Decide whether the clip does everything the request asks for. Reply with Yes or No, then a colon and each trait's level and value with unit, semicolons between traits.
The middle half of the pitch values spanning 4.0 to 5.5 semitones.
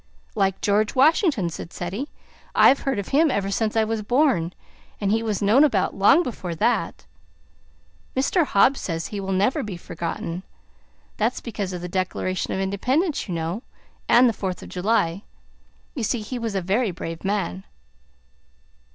Yes: average, 4.8 semitones